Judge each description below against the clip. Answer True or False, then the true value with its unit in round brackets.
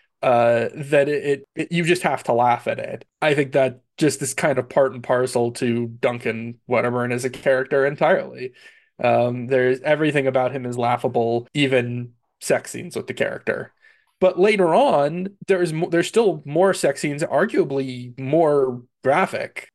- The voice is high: False (140 Hz)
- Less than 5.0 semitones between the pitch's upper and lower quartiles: False (5.6 semitones)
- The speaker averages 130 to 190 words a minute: True (170 wpm)